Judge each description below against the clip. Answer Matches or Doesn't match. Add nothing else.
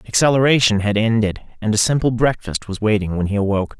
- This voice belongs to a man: Matches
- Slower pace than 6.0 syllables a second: Doesn't match